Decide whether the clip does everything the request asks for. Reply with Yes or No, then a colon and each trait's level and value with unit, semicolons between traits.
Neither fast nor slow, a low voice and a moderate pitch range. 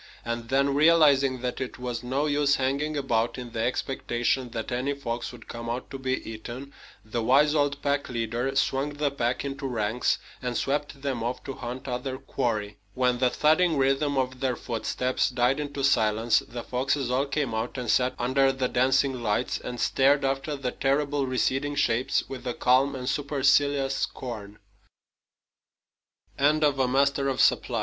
No: average, 145 wpm; low, 130 Hz; narrow, 2.3 semitones